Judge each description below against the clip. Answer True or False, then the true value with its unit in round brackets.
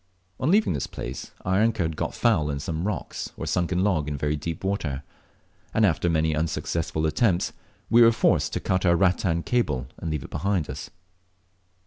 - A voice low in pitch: True (85 Hz)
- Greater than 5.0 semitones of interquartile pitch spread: False (4.4 semitones)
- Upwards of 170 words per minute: True (185 wpm)